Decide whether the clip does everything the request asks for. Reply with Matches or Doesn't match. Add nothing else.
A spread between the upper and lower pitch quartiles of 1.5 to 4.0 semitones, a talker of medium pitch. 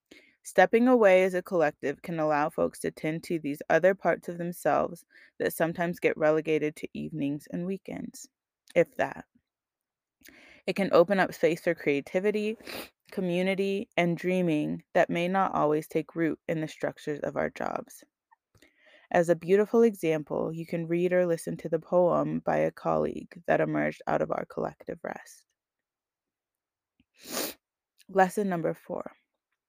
Matches